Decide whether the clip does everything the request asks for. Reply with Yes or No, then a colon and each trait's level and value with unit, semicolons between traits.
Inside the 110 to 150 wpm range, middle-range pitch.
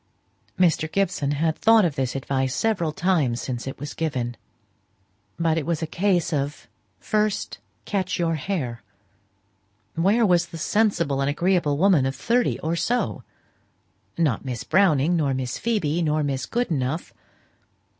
Yes: average, 145 wpm; medium, 160 Hz